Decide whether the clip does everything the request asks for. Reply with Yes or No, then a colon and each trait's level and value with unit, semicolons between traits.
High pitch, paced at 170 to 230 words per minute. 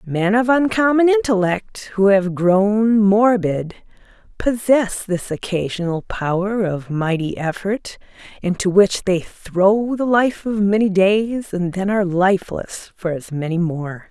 No: high, 200 Hz; slow, 135 wpm